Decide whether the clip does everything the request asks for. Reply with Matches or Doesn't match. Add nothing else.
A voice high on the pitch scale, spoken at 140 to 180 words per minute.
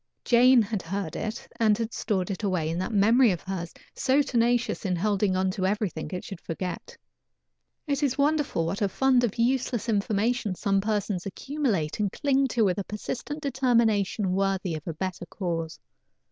Matches